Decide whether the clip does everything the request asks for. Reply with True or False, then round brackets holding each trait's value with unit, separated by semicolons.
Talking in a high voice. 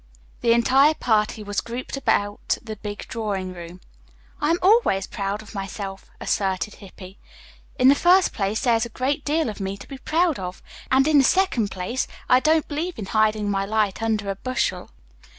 True (220 Hz)